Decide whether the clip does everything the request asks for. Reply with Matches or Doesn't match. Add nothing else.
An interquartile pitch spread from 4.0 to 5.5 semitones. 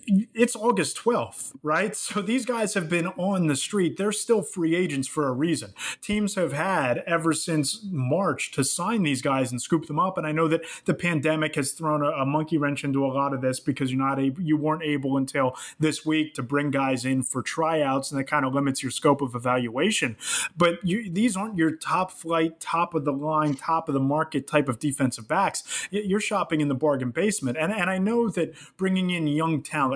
Matches